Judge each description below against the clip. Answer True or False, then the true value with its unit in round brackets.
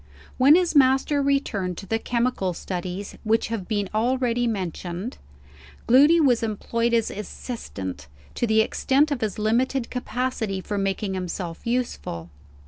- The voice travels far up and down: False (4.7 semitones)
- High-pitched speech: True (225 Hz)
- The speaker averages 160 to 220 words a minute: False (135 wpm)